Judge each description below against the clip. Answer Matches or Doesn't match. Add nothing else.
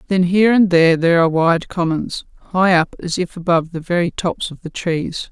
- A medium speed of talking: Doesn't match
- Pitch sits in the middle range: Matches